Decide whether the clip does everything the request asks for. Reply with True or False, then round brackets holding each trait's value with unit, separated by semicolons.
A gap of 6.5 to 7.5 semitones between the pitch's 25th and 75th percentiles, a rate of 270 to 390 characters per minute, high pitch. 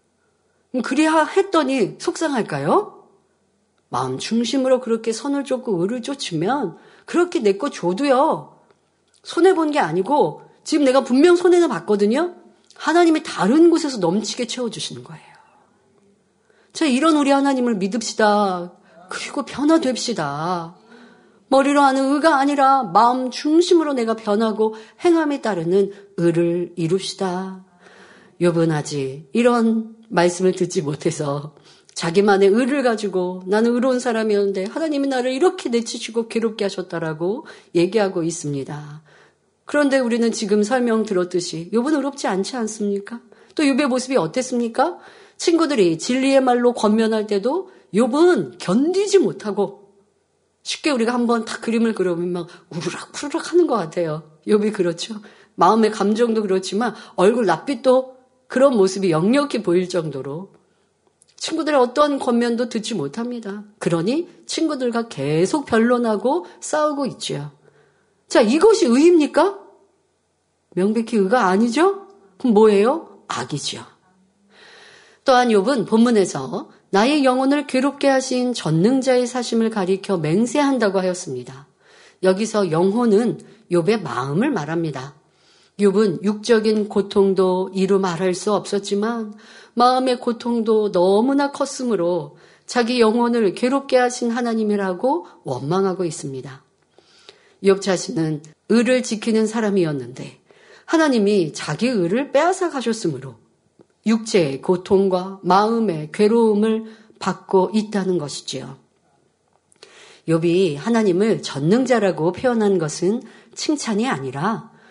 False (5.8 semitones; 290 characters per minute; 220 Hz)